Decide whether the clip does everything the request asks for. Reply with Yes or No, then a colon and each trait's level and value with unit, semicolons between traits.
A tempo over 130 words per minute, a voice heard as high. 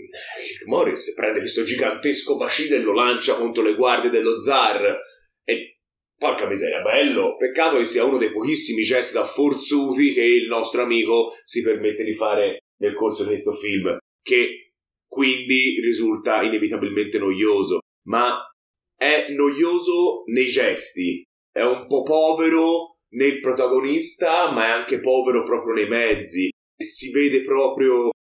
Yes: average, 140 wpm; very high, 355 Hz